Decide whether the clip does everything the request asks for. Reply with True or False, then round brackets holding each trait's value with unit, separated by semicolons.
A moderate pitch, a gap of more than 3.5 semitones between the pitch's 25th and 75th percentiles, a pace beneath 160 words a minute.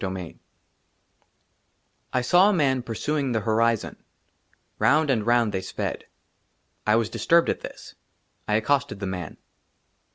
False (115 Hz; 5.1 semitones; 135 wpm)